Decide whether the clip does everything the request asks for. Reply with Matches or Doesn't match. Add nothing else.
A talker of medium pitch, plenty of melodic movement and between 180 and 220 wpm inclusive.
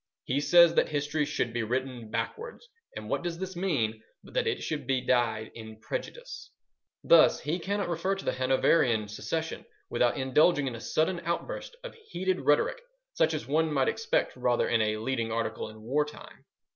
Matches